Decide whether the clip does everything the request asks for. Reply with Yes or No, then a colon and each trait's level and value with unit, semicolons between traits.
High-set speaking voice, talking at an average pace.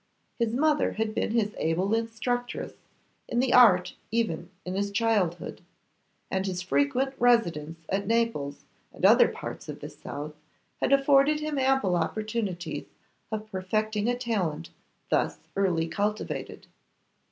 No: high, 215 Hz; slow, 130 wpm